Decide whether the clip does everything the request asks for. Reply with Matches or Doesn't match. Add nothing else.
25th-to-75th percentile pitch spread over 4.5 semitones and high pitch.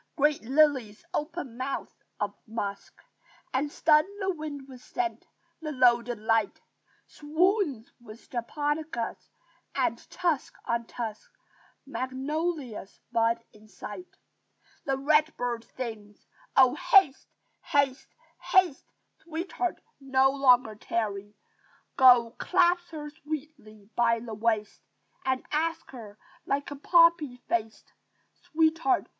Matches